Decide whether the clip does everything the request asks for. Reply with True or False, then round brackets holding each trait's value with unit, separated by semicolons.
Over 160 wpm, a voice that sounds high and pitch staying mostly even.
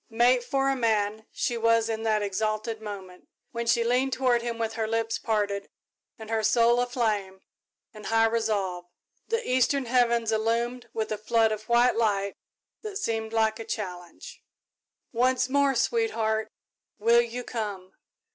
False (155 wpm; 225 Hz; 2.0 semitones)